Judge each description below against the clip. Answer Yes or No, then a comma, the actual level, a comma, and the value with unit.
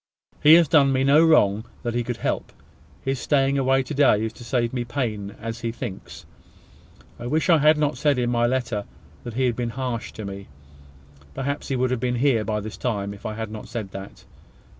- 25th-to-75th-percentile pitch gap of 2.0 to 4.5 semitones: Yes, average, 3.5 semitones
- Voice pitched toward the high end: No, low, 120 Hz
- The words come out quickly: Yes, fast, 220 wpm